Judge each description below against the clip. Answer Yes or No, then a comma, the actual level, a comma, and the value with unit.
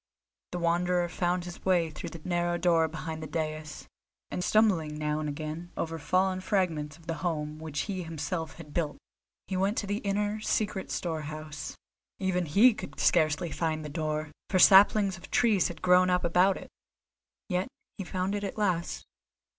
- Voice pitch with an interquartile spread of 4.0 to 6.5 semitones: No, average, 3.1 semitones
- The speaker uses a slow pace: No, average, 175 wpm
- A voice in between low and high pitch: Yes, medium, 175 Hz